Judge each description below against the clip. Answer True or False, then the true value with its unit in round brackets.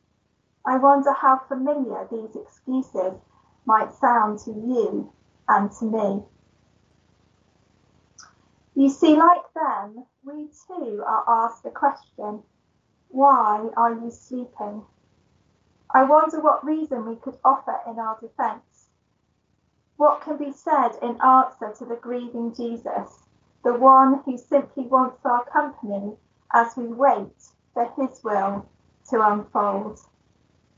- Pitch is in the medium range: False (255 Hz)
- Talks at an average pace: False (120 wpm)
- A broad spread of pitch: False (3.8 semitones)